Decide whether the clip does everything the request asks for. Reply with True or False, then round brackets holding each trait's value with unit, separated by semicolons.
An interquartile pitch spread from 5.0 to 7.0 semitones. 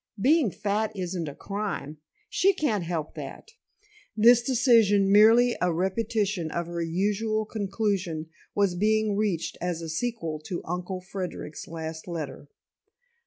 False (4.3 semitones)